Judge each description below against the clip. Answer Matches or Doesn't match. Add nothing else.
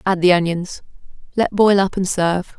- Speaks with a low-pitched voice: Doesn't match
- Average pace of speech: Matches